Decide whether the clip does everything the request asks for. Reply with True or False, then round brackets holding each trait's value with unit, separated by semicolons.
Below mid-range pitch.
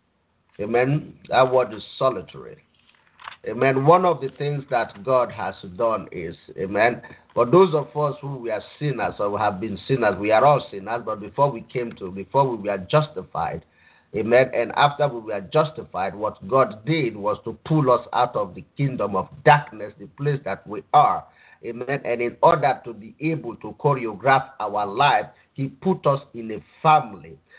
True (130 Hz)